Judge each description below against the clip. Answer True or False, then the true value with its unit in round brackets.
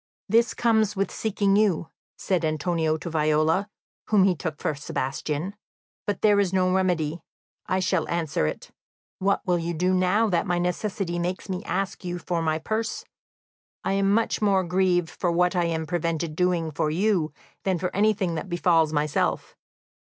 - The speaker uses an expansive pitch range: False (3.2 semitones)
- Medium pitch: True (180 Hz)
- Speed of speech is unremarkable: True (170 wpm)